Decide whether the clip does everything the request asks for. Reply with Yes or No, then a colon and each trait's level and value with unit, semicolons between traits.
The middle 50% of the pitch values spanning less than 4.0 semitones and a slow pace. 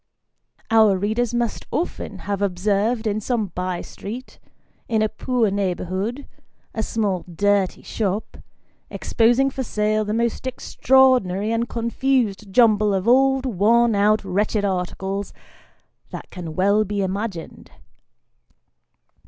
Yes: average, 3.1 semitones; slow, 120 wpm